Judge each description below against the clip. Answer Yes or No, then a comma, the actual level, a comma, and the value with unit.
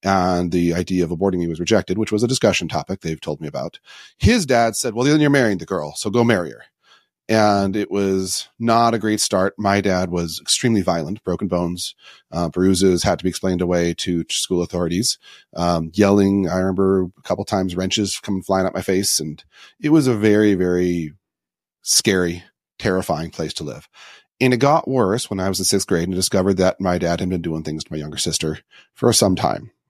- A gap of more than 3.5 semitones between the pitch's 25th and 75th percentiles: No, average, 2.8 semitones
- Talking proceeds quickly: Yes, fast, 210 wpm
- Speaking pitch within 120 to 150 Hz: No, very low, 95 Hz